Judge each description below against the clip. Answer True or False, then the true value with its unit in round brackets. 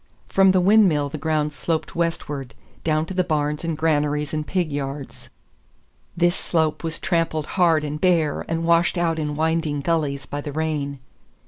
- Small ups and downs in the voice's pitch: True (2.2 semitones)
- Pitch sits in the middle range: True (155 Hz)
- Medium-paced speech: True (165 wpm)